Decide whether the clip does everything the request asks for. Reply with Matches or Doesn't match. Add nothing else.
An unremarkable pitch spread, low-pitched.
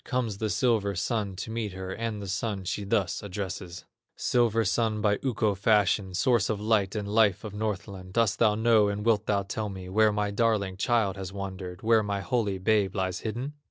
Doesn't match